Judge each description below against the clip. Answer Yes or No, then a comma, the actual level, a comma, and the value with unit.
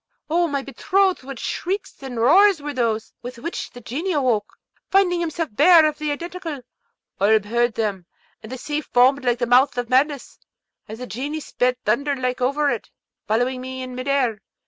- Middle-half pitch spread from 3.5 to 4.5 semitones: Yes, average, 3.9 semitones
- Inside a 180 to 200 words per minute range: Yes, average, 185 wpm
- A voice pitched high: Yes, very high, 265 Hz